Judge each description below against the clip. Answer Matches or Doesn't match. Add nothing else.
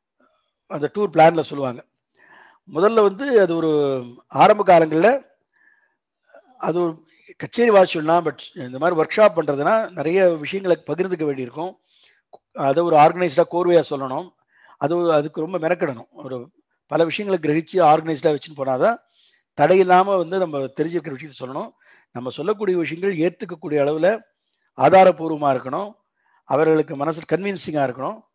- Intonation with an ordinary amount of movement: Matches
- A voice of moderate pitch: Matches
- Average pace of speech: Matches